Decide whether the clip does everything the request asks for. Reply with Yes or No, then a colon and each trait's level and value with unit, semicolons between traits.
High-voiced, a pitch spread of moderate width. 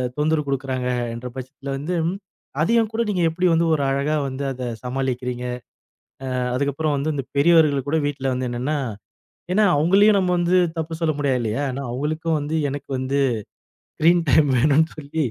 No: medium, 145 Hz; average, 3.5 semitones